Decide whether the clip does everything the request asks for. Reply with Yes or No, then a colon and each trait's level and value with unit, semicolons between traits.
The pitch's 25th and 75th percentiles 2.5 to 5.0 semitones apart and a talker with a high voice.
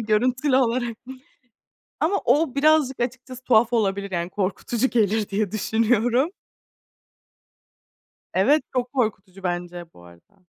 Yes: average, 4.6 semitones; high, 230 Hz